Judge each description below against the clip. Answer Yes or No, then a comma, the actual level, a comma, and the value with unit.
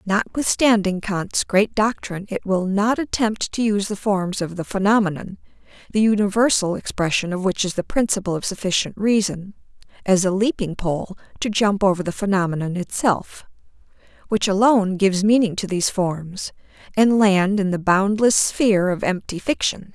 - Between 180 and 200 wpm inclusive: No, average, 155 wpm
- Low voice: No, high, 200 Hz